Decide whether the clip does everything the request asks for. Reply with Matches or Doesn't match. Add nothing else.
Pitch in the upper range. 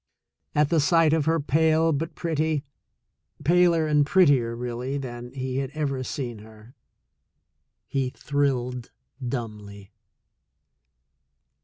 Doesn't match